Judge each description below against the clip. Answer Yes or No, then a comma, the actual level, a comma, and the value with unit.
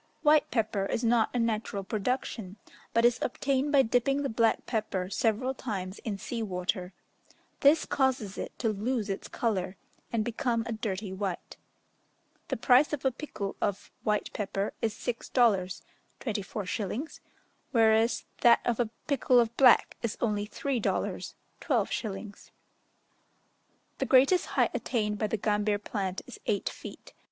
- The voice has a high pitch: Yes, high, 225 Hz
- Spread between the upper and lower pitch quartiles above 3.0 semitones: Yes, average, 3.4 semitones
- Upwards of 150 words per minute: No, average, 145 wpm